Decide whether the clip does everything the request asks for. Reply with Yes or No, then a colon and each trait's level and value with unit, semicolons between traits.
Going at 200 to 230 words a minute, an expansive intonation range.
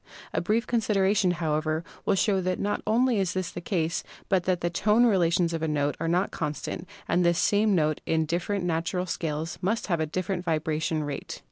No: fast, 205 wpm; average, 3.3 semitones